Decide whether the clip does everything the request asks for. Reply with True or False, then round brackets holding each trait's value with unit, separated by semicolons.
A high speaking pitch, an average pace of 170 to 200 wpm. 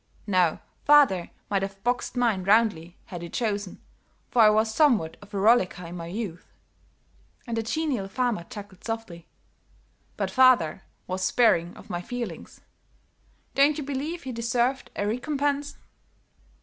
False (220 Hz; 145 wpm)